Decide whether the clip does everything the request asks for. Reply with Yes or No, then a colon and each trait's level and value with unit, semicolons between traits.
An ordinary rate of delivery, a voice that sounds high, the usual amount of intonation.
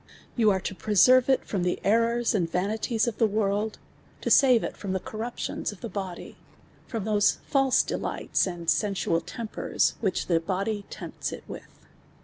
Yes: average, 175 wpm; high, 210 Hz; average, 3.4 semitones